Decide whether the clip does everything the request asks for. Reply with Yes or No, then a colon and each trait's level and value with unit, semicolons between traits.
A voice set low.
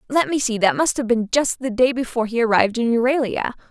No: high, 240 Hz